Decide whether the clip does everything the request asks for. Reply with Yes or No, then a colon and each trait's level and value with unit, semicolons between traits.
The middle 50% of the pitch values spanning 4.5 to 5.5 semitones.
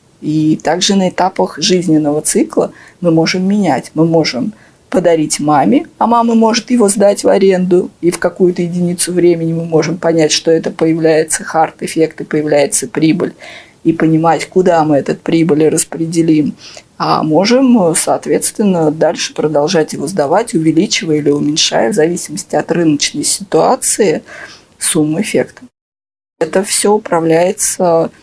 No: average, 3.2 semitones